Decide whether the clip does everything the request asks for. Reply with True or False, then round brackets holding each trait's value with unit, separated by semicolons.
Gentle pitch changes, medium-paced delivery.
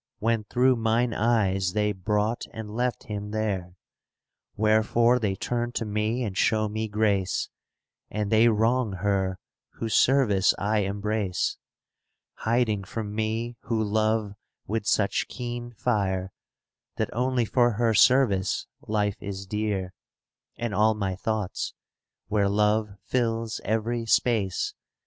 False (2.2 semitones; 130 wpm)